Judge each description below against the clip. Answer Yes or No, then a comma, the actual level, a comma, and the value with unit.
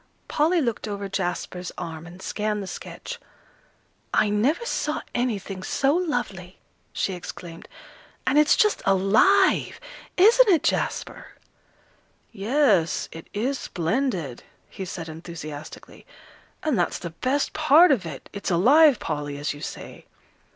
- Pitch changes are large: Yes, wide, 8.7 semitones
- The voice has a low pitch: No, high, 205 Hz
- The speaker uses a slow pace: Yes, slow, 130 wpm